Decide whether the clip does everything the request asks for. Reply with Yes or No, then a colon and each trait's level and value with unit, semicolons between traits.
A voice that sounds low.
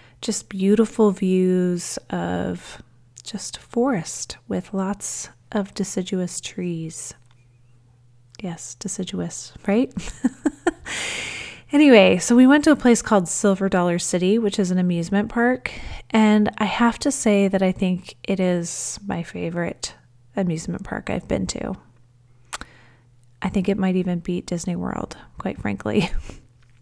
No: medium, 185 Hz